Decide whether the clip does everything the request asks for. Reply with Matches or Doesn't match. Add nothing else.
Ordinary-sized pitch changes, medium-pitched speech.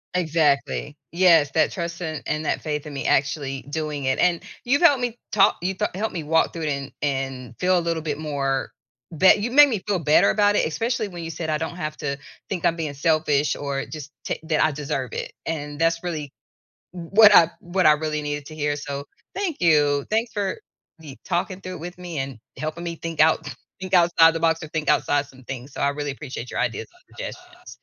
Matches